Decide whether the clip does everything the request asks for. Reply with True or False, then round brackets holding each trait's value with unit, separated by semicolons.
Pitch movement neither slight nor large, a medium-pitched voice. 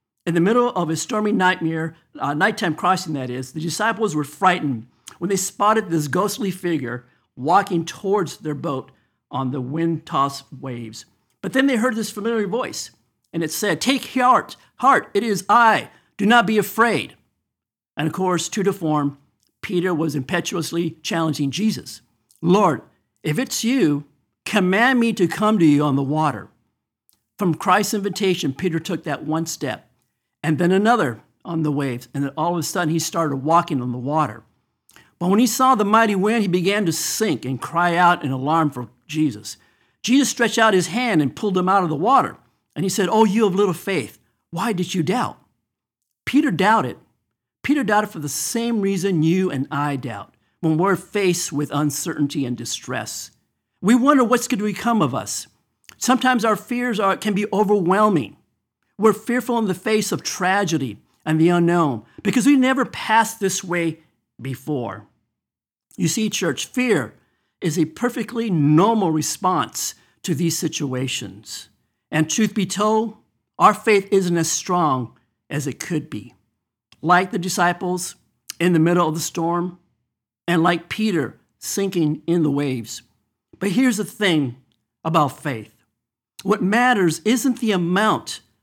False (6.1 semitones; 175 Hz)